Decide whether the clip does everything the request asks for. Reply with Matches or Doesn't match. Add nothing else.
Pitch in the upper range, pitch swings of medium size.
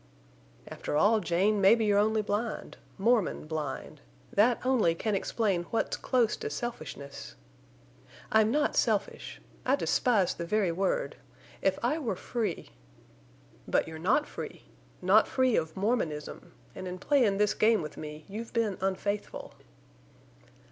Matches